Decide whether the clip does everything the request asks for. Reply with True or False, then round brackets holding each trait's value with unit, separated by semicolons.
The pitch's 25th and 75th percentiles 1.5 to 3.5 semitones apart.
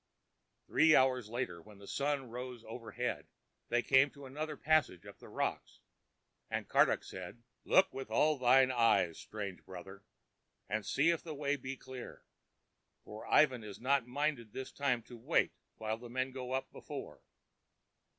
False (4.0 semitones)